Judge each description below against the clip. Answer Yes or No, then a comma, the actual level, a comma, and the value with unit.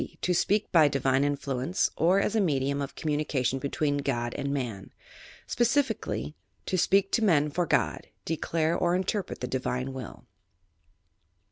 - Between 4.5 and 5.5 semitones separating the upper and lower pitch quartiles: Yes, average, 5.1 semitones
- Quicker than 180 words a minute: No, average, 145 wpm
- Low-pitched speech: No, medium, 150 Hz